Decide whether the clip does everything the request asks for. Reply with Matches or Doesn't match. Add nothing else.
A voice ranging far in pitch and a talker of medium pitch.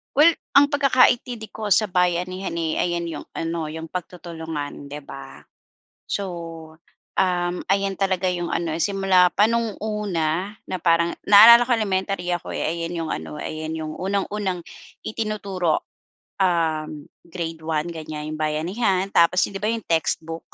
Doesn't match